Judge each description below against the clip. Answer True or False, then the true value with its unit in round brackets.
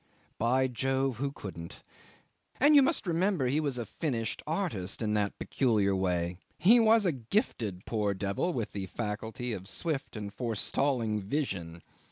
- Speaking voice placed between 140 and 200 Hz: False (120 Hz)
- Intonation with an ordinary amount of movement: False (6.6 semitones)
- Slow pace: False (155 wpm)